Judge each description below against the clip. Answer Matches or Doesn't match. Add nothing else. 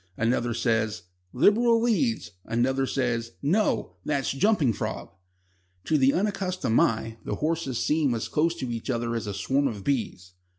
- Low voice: Matches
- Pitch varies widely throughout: Matches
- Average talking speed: Matches